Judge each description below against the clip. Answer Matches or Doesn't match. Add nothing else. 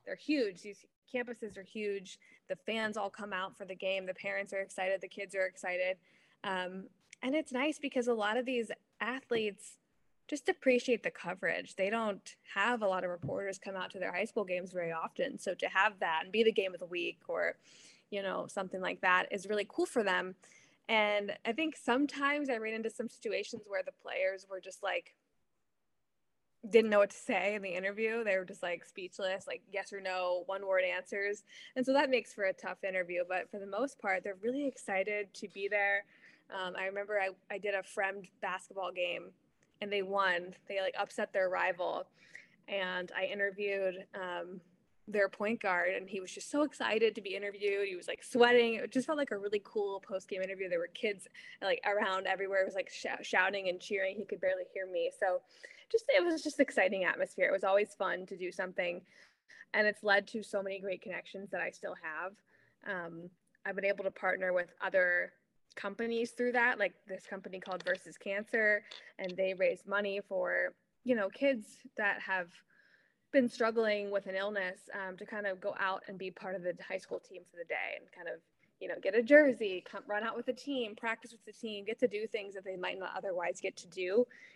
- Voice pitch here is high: Matches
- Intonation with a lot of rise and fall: Doesn't match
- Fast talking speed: Matches